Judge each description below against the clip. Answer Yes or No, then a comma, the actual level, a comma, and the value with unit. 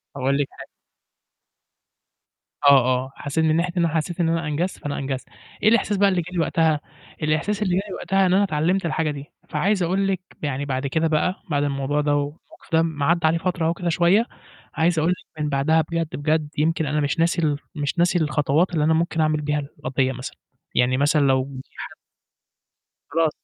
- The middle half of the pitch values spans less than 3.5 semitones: Yes, average, 2.9 semitones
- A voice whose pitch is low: No, medium, 160 Hz